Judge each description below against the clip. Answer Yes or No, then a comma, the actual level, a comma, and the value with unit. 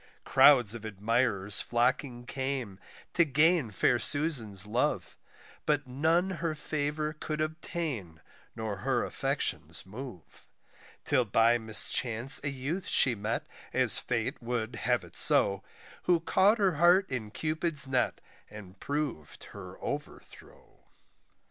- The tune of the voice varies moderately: No, wide, 5.7 semitones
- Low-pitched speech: Yes, low, 130 Hz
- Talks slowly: Yes, slow, 125 wpm